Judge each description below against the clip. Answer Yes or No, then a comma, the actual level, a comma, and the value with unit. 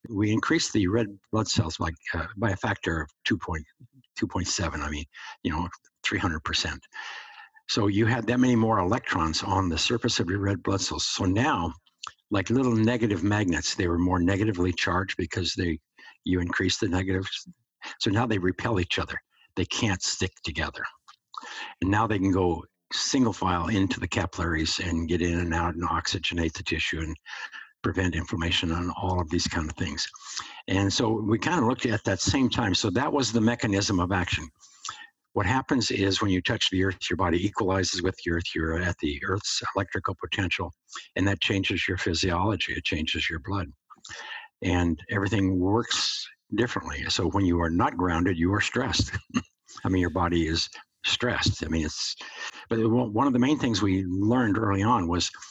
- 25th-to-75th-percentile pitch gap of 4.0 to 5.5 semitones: Yes, average, 4.5 semitones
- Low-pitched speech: Yes, very low, 95 Hz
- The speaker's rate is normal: Yes, average, 190 wpm